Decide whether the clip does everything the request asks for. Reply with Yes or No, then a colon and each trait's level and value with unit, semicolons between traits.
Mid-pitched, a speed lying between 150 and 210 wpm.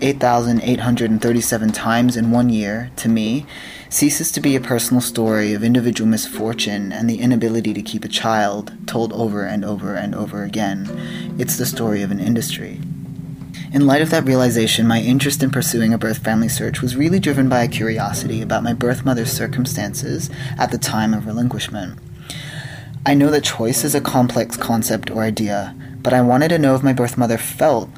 No: low, 120 Hz; average, 180 wpm